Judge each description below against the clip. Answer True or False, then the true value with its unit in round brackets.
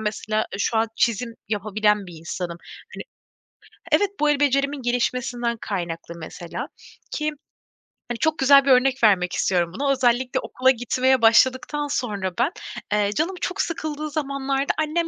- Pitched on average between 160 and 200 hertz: False (250 Hz)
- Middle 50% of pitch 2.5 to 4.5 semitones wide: False (5.0 semitones)